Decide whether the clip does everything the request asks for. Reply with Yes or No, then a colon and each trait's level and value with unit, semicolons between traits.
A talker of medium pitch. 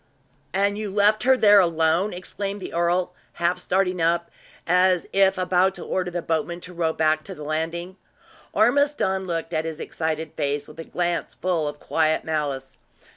Yes: medium, 175 Hz